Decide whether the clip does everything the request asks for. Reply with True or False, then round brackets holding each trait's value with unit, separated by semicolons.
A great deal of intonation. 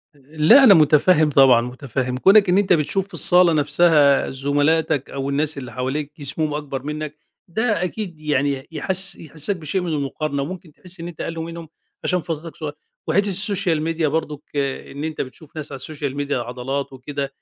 False (3.3 semitones)